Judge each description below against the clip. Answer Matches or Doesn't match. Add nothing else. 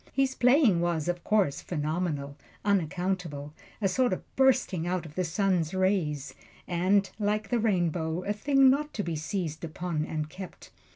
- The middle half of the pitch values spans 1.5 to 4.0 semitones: Doesn't match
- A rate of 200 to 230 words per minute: Doesn't match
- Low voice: Doesn't match